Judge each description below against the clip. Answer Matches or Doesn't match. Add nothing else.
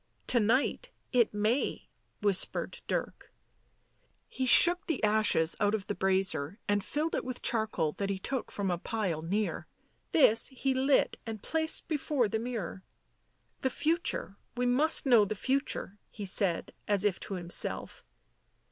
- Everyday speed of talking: Matches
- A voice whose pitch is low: Doesn't match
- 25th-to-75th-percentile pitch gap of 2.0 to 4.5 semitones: Doesn't match